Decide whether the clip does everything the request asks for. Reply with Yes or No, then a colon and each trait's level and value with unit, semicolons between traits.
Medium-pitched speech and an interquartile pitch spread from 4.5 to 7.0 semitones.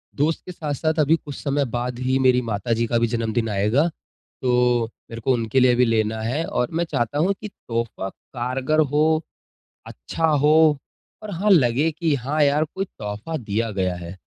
No: low, 130 Hz; average, 5.0 semitones